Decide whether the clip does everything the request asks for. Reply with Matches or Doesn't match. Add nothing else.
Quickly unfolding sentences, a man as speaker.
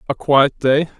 Doesn't match